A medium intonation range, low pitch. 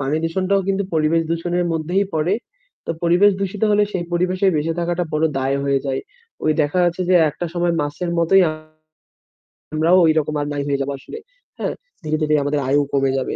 No: average, 3.4 semitones; medium, 165 Hz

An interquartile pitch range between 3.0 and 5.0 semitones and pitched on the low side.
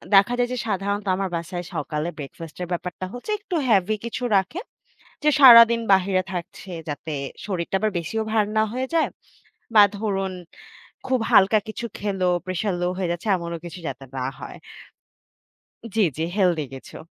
No: average, 4.1 semitones; high, 195 Hz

